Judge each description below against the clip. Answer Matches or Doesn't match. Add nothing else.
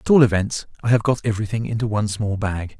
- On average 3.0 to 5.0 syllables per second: Doesn't match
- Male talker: Matches